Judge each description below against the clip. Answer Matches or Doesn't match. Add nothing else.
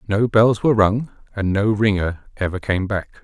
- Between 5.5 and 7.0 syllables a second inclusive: Doesn't match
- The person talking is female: Doesn't match